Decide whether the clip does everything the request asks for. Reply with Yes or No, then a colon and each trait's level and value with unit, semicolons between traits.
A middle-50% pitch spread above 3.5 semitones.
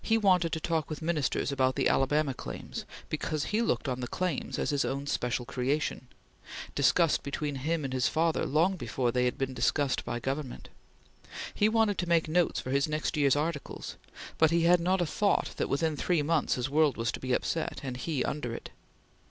Yes: average, 4.1 semitones